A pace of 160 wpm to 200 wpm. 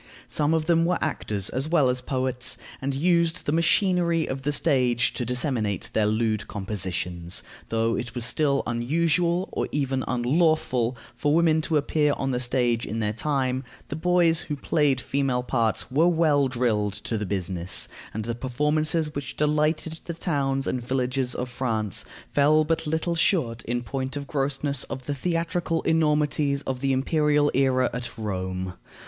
Yes: average, 165 wpm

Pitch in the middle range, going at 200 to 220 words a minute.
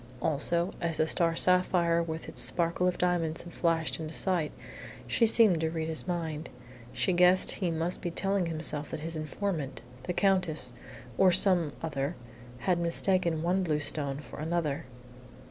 No: medium, 170 Hz; average, 165 wpm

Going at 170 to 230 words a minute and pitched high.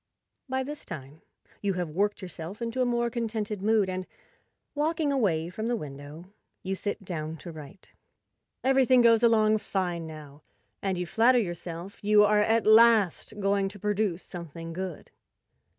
No: average, 160 wpm; high, 200 Hz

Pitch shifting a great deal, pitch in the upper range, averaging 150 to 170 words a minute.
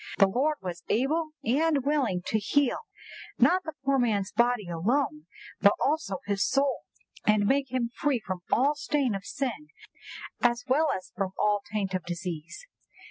Yes: wide, 6.3 semitones; high, 240 Hz; average, 160 wpm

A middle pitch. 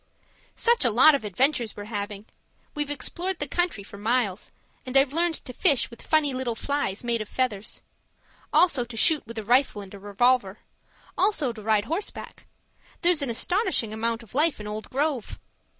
No: high, 245 Hz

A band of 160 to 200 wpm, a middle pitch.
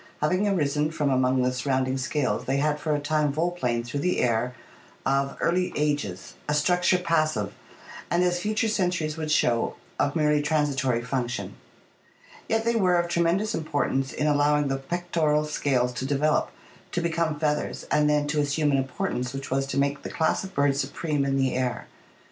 Yes: average, 180 wpm; medium, 150 Hz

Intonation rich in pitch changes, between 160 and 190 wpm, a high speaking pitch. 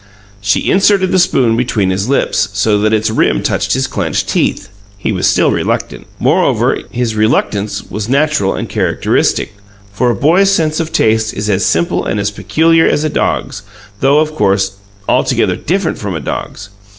No: wide, 7.0 semitones; average, 175 wpm; low, 110 Hz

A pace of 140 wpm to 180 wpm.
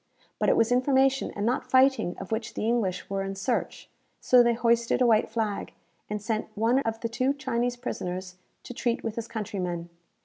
No: average, 195 wpm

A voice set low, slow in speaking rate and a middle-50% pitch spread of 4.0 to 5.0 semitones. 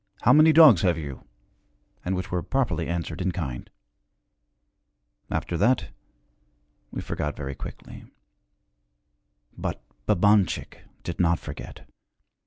Yes: very low, 90 Hz; slow, 110 wpm; average, 4.4 semitones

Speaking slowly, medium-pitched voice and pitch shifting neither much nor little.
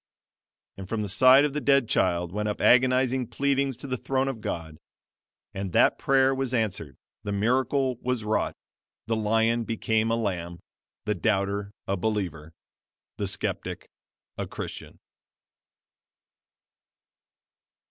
No: slow, 130 wpm; low, 110 Hz; average, 4.6 semitones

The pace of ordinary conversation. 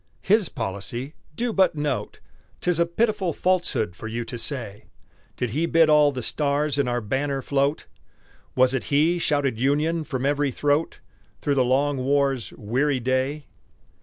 Yes: average, 160 wpm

